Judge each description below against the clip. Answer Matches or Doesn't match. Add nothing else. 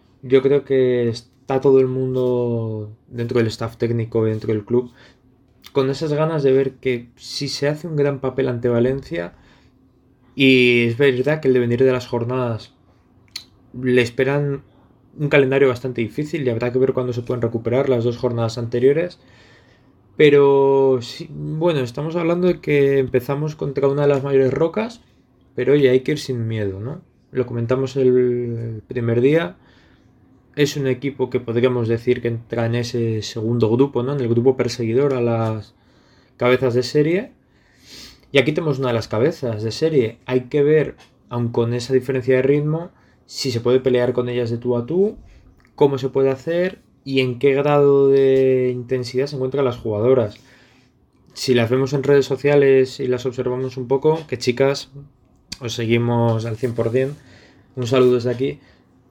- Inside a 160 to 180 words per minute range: Matches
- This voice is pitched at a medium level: Doesn't match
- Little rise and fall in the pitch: Matches